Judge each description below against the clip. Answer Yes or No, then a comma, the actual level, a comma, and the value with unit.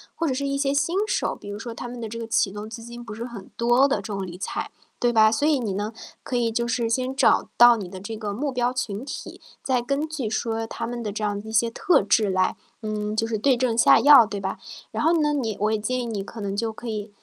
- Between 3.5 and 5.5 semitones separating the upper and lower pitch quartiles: No, average, 3.0 semitones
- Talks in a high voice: Yes, high, 230 Hz